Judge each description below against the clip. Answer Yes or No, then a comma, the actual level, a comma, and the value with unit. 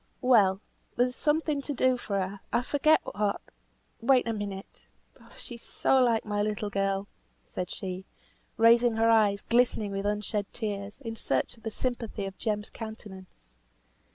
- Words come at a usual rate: Yes, average, 155 wpm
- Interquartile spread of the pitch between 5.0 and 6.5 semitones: No, average, 3.3 semitones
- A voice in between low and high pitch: No, high, 215 Hz